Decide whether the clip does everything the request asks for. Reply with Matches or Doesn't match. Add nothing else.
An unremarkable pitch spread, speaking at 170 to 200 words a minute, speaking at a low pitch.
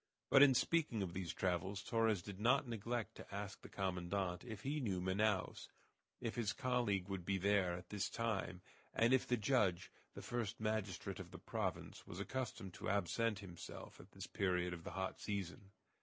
Matches